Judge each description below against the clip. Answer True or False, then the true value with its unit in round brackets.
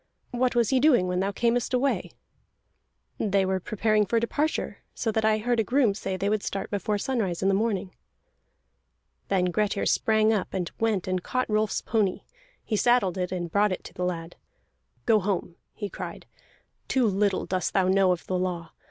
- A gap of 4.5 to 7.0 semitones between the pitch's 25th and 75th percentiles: False (3.3 semitones)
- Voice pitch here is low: False (205 Hz)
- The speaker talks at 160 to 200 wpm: True (185 wpm)